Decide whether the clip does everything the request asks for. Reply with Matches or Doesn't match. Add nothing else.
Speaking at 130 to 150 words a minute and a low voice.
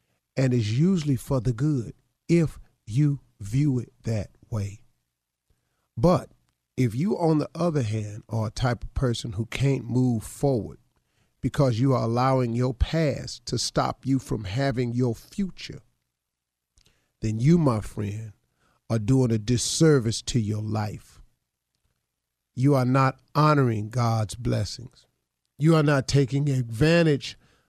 Matches